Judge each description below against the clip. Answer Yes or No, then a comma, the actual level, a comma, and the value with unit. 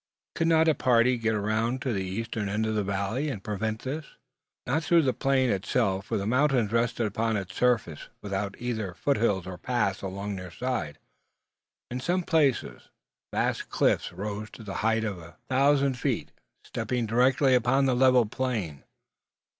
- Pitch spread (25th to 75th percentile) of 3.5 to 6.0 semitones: Yes, average, 4.4 semitones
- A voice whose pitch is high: No, low, 115 Hz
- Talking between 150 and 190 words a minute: Yes, average, 170 wpm